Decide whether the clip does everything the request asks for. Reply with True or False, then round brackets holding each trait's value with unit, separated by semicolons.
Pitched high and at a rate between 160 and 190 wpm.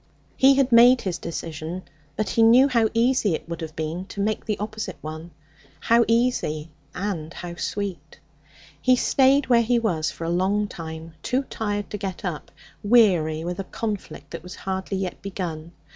True (195 Hz; 175 wpm)